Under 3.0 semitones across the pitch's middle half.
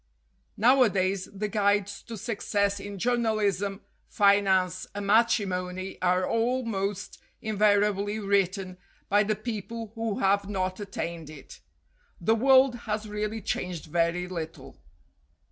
Yes: narrow, 2.5 semitones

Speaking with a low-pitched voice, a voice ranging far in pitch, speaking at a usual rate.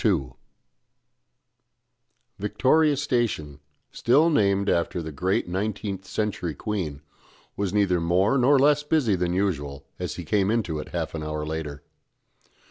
No: very low, 95 Hz; wide, 5.7 semitones; slow, 130 wpm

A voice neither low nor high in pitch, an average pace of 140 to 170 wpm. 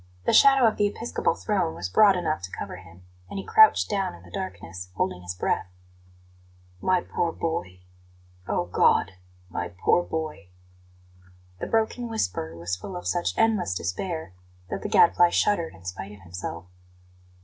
No: low, 105 Hz; average, 160 wpm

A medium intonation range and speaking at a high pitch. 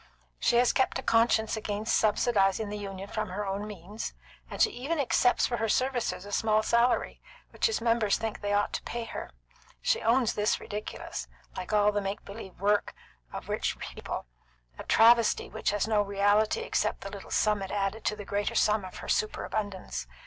No: narrow, 2.1 semitones; high, 210 Hz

